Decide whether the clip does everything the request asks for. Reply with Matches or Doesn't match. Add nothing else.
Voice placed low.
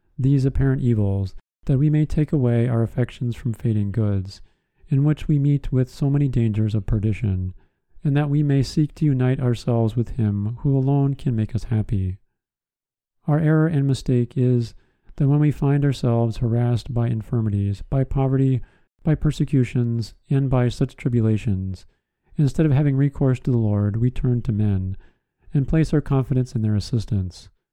Matches